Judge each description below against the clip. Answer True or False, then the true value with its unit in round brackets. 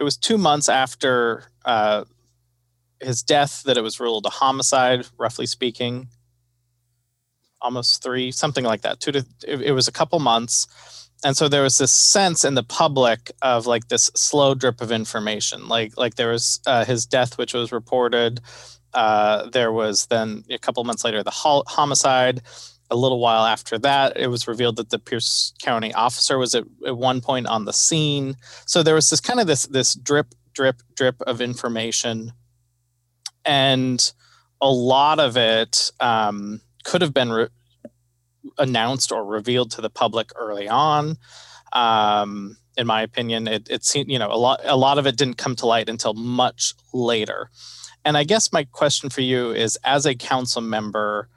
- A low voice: True (120 Hz)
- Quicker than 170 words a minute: True (180 wpm)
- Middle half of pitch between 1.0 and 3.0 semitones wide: True (2.5 semitones)